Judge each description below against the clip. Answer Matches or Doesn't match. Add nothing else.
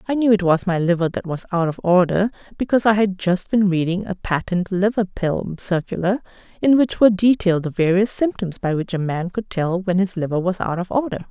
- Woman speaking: Matches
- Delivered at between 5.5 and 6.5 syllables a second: Matches